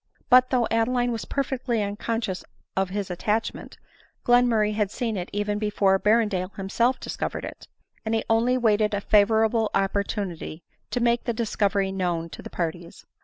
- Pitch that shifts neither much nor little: Yes, average, 3.2 semitones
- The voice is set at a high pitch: Yes, high, 210 Hz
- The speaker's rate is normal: Yes, average, 160 wpm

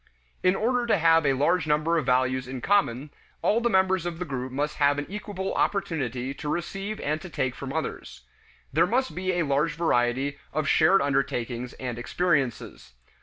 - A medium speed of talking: Yes, average, 180 wpm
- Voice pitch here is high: No, medium, 155 Hz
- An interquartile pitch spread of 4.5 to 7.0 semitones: Yes, wide, 5.6 semitones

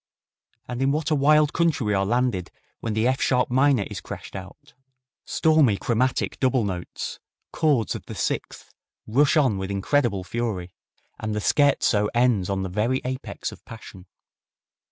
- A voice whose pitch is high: No, low, 120 Hz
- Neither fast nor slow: Yes, average, 160 wpm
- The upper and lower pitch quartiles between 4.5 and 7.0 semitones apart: Yes, wide, 5.5 semitones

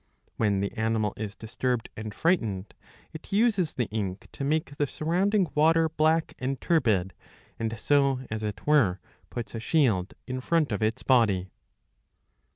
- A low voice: Yes, low, 125 Hz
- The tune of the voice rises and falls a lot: Yes, wide, 6.5 semitones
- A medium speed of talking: Yes, average, 160 wpm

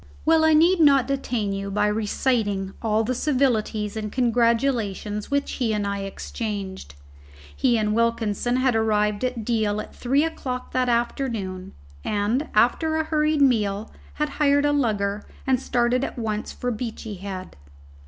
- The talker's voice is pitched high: Yes, high, 230 Hz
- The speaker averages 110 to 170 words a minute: Yes, average, 155 wpm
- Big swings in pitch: No, average, 4.0 semitones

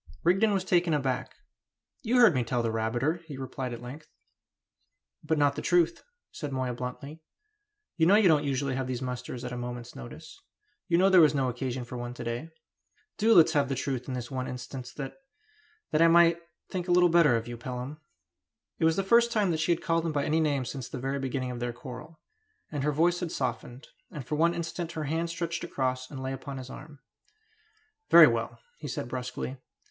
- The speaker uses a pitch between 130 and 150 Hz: Yes, medium, 140 Hz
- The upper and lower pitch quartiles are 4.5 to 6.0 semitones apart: Yes, average, 4.8 semitones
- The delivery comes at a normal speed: No, fast, 215 wpm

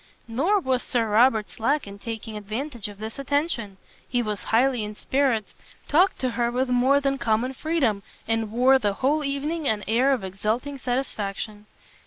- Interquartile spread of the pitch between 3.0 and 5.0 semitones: Yes, average, 4.1 semitones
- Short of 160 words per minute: No, average, 170 wpm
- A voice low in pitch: No, high, 245 Hz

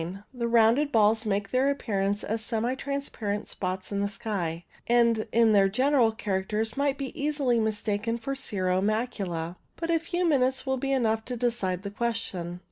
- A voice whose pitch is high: Yes, high, 225 Hz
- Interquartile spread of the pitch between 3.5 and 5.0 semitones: Yes, average, 4.2 semitones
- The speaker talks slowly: No, average, 175 wpm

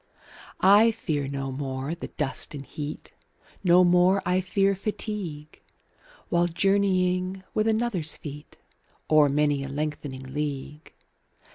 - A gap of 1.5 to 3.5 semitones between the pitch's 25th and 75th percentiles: No, average, 4.7 semitones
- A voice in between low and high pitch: Yes, medium, 165 Hz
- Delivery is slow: Yes, slow, 125 wpm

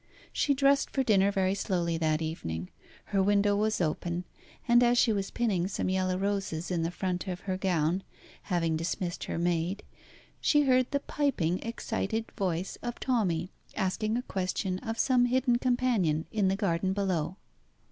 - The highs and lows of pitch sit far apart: No, average, 4.7 semitones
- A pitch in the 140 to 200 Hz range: Yes, high, 190 Hz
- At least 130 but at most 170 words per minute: Yes, average, 165 wpm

